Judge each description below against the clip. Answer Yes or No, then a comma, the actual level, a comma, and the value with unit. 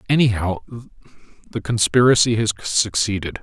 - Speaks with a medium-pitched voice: No, low, 105 Hz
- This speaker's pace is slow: Yes, slow, 90 wpm